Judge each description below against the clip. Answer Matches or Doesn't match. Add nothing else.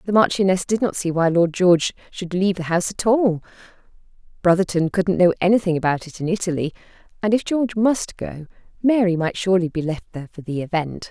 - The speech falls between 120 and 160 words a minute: Doesn't match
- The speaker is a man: Doesn't match